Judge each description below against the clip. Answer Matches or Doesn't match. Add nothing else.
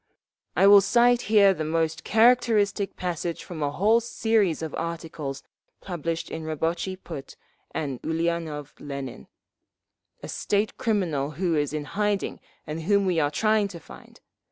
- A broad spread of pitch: Doesn't match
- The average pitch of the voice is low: Doesn't match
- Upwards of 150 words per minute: Doesn't match